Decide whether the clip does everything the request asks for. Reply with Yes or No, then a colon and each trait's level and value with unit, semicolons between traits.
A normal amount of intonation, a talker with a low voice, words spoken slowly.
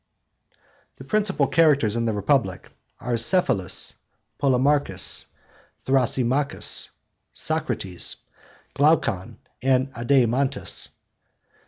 Yes: average, 3.8 semitones; low, 130 Hz; slow, 70 wpm